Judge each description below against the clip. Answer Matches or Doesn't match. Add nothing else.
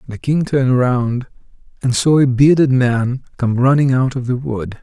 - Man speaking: Matches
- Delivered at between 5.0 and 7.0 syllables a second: Doesn't match